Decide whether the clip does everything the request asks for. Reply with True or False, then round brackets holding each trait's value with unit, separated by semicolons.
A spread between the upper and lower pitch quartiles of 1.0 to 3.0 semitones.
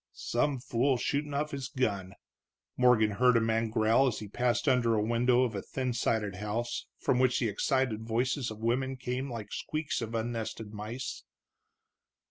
True (2.7 semitones)